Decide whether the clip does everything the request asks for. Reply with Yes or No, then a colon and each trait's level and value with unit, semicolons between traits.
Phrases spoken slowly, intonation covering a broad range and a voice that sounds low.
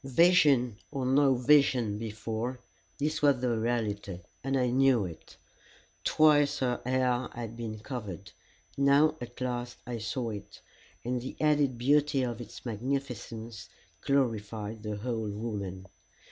No: slow, 130 wpm; average, 3.6 semitones; low, 120 Hz